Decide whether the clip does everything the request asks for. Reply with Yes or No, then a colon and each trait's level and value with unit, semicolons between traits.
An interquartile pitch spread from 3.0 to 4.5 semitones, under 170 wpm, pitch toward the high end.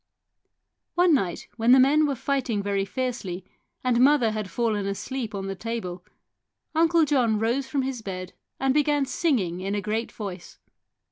No: average, 5.3 semitones; average, 160 wpm; high, 230 Hz